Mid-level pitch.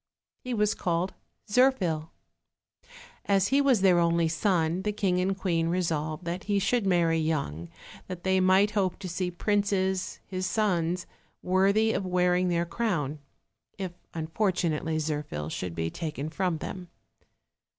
Yes: medium, 180 Hz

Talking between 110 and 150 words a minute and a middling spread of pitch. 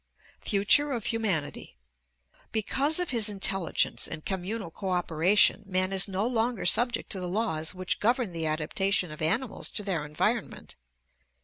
Yes: average, 140 wpm; average, 4.3 semitones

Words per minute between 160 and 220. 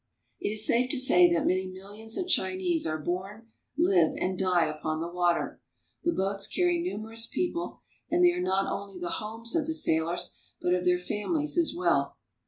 Yes: average, 190 wpm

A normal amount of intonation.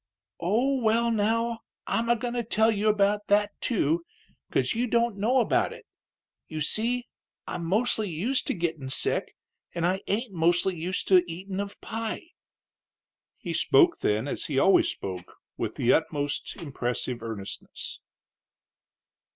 No: wide, 5.9 semitones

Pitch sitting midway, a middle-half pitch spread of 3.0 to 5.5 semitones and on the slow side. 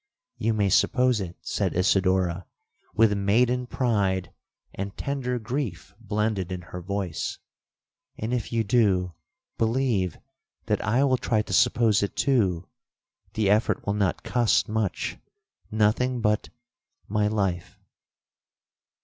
No: low, 105 Hz; average, 3.7 semitones; slow, 115 wpm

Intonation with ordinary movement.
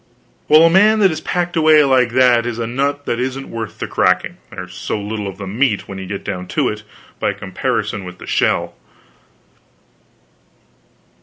No: wide, 6.7 semitones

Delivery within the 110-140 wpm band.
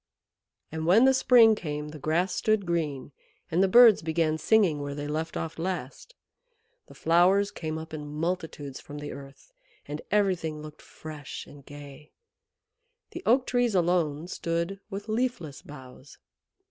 No: average, 150 wpm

